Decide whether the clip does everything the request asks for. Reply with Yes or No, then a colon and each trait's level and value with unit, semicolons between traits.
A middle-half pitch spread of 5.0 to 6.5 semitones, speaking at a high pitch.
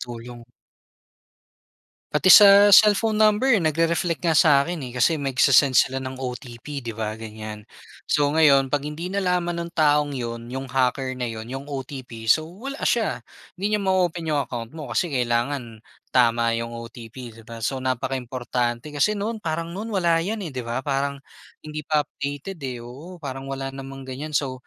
No: average, 5.3 semitones; medium, 140 Hz